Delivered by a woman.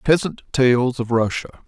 No: male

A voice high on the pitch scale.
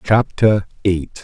No: low, 100 Hz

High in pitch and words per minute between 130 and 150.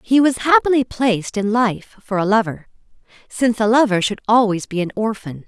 No: high, 225 Hz; average, 185 wpm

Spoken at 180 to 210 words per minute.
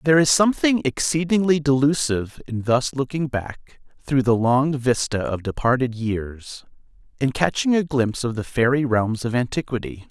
No: average, 155 wpm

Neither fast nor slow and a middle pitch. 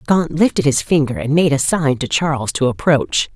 No: fast, 215 wpm; medium, 145 Hz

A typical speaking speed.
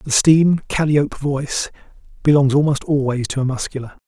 Yes: average, 145 wpm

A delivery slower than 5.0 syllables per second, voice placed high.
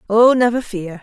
Yes: 4.7 syllables/s; high, 220 Hz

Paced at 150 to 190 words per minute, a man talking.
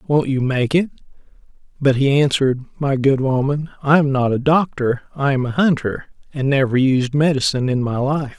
Yes: average, 185 wpm; male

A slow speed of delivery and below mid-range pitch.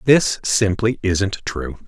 Yes: slow, 130 wpm; low, 100 Hz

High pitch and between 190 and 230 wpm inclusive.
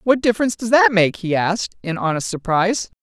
Yes: high, 200 Hz; average, 200 wpm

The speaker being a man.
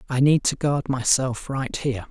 Yes: male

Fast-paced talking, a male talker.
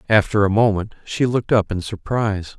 No: average, 185 wpm; male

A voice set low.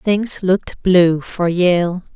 No: medium, 185 Hz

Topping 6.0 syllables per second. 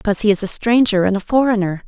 Yes: 7.1 syllables/s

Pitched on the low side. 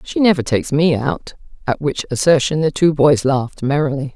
No: medium, 150 Hz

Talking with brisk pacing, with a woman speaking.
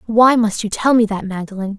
Yes: fast, 235 wpm; female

